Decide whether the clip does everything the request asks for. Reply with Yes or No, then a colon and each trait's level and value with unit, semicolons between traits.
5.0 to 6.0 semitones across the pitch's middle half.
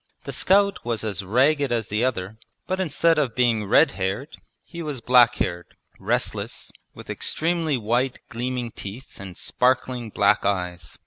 Yes: wide, 5.4 semitones